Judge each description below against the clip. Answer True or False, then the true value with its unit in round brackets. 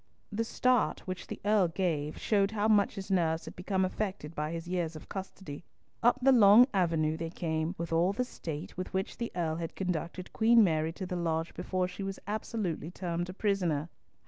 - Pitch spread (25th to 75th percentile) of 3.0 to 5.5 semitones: True (3.5 semitones)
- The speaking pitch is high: False (180 Hz)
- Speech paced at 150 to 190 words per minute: False (200 wpm)